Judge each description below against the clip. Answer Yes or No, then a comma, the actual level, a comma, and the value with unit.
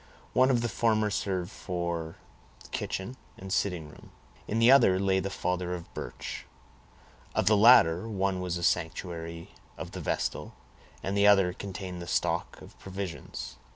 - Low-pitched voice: Yes, very low, 95 Hz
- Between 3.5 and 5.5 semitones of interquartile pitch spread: No, average, 2.7 semitones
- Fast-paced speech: No, average, 155 wpm